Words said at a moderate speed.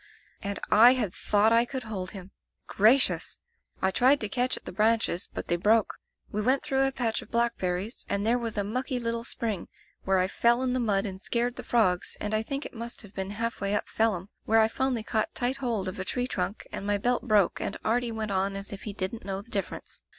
No: fast, 240 wpm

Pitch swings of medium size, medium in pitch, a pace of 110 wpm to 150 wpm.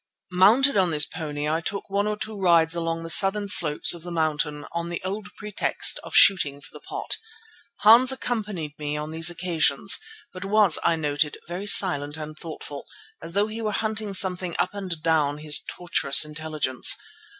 No: average, 4.7 semitones; medium, 170 Hz; average, 180 wpm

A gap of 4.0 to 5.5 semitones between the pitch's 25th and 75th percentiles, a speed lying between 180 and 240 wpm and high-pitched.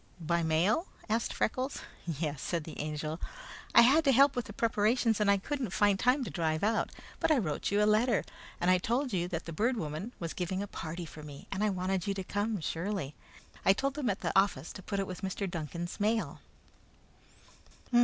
Yes: average, 5.0 semitones; fast, 205 wpm; high, 195 Hz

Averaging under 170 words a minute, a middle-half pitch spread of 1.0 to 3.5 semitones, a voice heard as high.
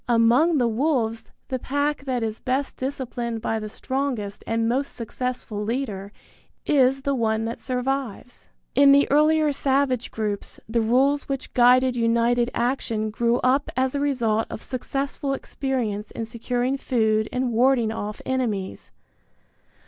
Yes: average, 140 wpm; average, 3.2 semitones; high, 245 Hz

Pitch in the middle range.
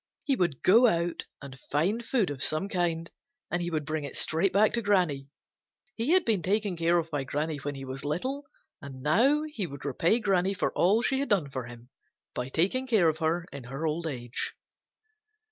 Yes: medium, 170 Hz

